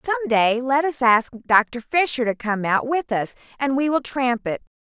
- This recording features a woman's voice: Yes, female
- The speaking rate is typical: No, fast, 210 wpm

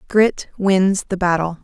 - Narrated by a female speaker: Yes, female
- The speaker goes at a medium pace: Yes, average, 145 wpm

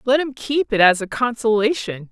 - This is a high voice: Yes, high, 235 Hz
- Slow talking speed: No, average, 200 wpm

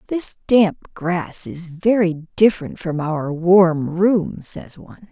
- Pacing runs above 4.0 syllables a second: No, 3.5 syllables/s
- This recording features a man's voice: No, female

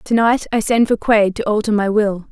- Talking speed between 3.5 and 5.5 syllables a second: Yes, 5.1 syllables/s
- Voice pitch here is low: No, high, 215 Hz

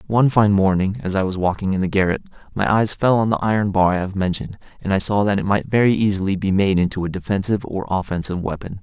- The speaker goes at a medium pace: No, fast, 245 wpm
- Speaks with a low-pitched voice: Yes, low, 100 Hz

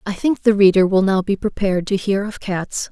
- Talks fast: Yes, fast, 245 wpm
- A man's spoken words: No, female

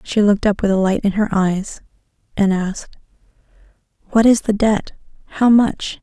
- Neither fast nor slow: Yes, average, 170 wpm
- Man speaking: No, female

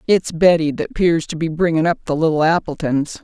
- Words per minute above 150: Yes, fast, 205 wpm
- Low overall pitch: No, medium, 165 Hz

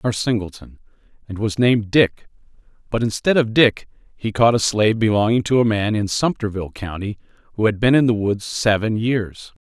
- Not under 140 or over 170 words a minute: No, average, 185 wpm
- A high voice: No, low, 110 Hz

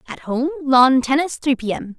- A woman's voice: Yes, female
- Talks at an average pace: No, fast, 210 wpm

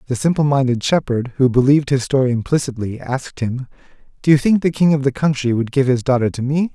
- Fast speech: Yes, fast, 220 wpm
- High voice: No, low, 135 Hz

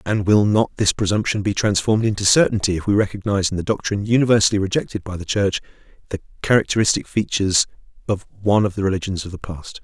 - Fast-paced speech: No, average, 190 wpm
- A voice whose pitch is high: No, low, 100 Hz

